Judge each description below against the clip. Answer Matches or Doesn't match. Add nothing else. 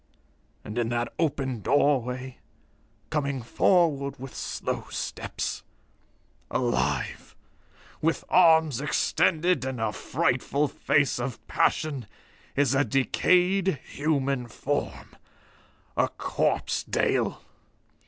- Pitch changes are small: Doesn't match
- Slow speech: Matches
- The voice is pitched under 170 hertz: Matches